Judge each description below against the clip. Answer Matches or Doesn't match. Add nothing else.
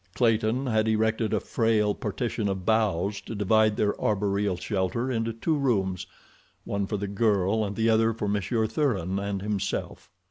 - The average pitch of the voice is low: Matches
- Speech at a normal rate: Matches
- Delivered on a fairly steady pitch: Matches